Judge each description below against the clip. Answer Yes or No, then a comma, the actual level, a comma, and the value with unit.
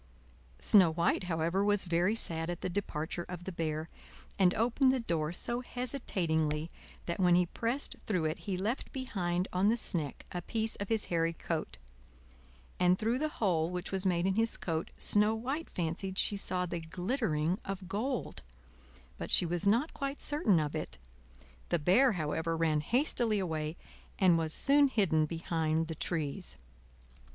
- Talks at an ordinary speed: Yes, average, 165 wpm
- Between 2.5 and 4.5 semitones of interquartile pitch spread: No, average, 5.0 semitones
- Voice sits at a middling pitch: Yes, medium, 180 Hz